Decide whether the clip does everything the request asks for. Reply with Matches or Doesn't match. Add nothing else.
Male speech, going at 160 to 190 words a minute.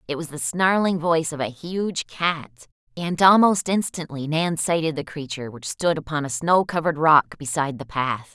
Doesn't match